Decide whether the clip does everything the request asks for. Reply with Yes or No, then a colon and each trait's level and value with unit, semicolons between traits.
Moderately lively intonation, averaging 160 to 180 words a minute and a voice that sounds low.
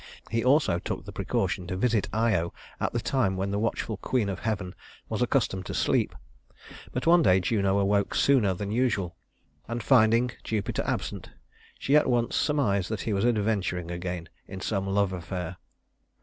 Yes: average, 3.8 semitones; average, 170 wpm; low, 100 Hz